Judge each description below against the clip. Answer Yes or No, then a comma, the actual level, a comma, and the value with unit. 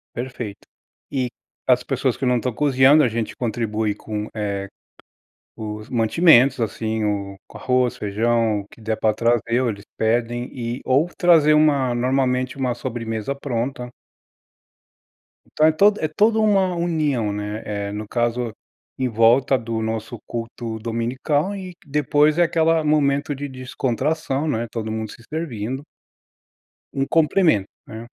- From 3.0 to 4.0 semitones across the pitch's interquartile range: No, average, 4.6 semitones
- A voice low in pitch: Yes, low, 125 Hz